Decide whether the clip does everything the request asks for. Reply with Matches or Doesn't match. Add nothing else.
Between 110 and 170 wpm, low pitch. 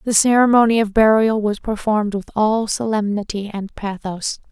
Doesn't match